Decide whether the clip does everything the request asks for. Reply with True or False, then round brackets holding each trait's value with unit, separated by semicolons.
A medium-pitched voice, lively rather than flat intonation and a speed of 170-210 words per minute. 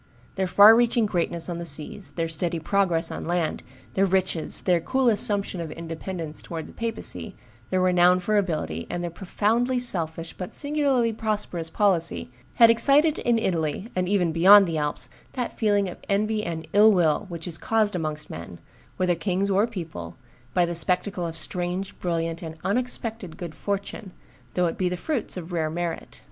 False (180 Hz; 4.0 semitones; 175 wpm)